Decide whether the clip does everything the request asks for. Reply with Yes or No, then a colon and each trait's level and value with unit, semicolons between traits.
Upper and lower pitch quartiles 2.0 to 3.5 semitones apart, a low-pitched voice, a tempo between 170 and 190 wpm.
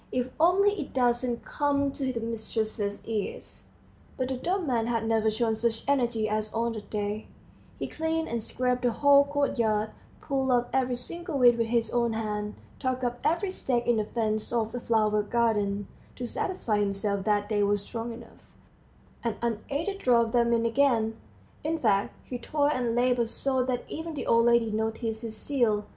No: average, 2.9 semitones; high, 235 Hz; average, 180 wpm